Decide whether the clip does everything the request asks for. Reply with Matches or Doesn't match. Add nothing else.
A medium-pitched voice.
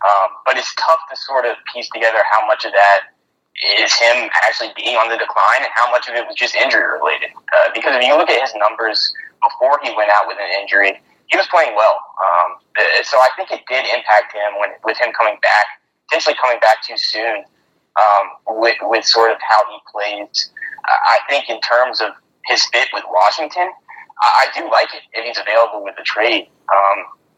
Matches